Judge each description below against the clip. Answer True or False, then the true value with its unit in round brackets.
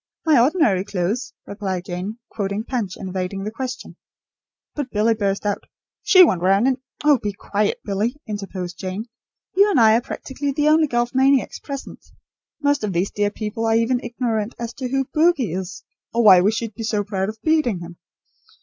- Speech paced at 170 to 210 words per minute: True (190 wpm)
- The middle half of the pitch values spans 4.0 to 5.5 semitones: True (4.9 semitones)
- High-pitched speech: True (220 Hz)